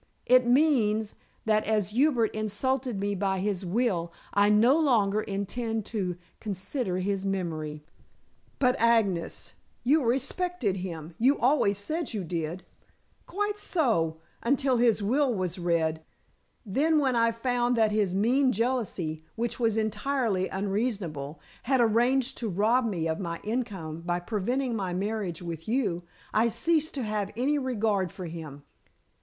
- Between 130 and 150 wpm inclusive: Yes, average, 145 wpm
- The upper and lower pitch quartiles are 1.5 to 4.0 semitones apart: No, average, 5.1 semitones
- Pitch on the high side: Yes, high, 215 Hz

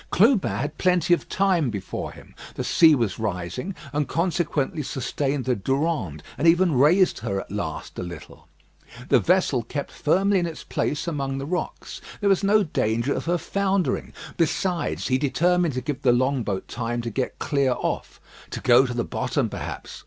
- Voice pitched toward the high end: No, medium, 145 Hz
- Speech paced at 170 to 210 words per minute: Yes, average, 180 wpm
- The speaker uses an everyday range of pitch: No, wide, 6.3 semitones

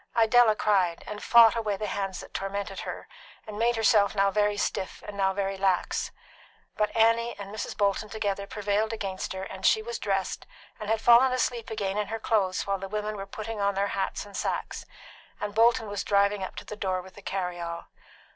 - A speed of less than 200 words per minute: No, fast, 205 wpm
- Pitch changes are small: Yes, narrow, 2.1 semitones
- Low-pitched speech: No, high, 205 Hz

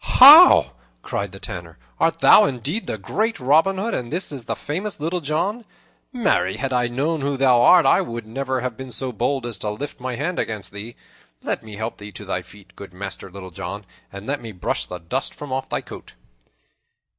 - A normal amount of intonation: No, wide, 6.3 semitones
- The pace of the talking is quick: Yes, fast, 210 wpm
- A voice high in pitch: No, low, 125 Hz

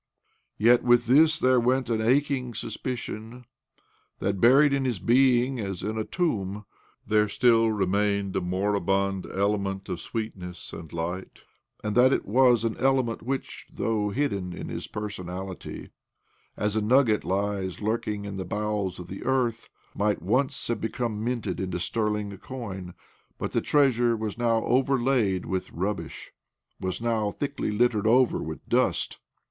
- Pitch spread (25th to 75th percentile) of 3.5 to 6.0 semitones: Yes, average, 3.8 semitones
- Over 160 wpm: No, average, 150 wpm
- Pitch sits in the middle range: No, low, 110 Hz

